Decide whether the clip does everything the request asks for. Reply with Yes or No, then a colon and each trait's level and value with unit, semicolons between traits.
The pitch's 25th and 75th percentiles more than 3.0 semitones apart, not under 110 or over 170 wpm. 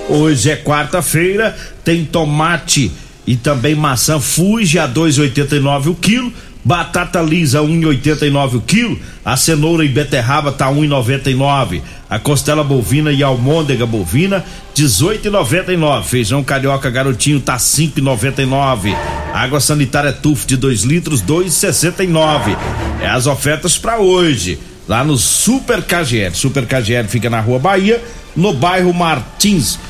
Yes: average, 3.8 semitones; average, 145 wpm